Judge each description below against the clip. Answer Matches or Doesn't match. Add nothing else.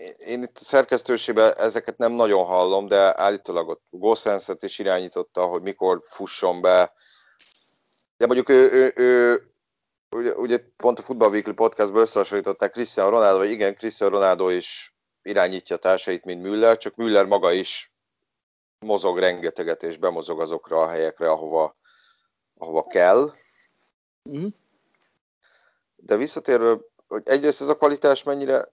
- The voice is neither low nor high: Doesn't match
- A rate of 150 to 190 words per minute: Doesn't match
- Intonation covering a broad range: Matches